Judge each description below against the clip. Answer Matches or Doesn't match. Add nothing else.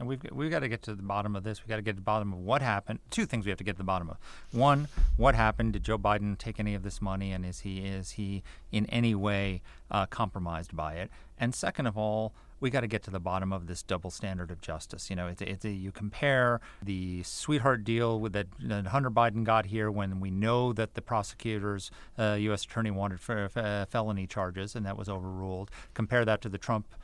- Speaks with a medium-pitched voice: Doesn't match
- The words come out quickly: Matches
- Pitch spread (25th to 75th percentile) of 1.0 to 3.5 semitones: Matches